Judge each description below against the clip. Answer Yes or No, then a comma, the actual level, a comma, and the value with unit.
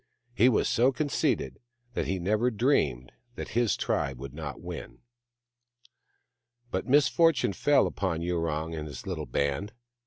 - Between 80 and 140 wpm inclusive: Yes, slow, 135 wpm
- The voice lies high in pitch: No, very low, 95 Hz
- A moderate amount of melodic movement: No, wide, 8.5 semitones